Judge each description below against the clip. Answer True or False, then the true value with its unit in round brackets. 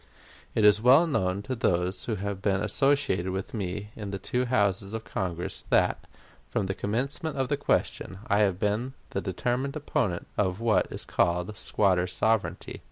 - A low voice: True (105 Hz)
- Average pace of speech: True (170 wpm)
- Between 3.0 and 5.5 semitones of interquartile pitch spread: True (4.7 semitones)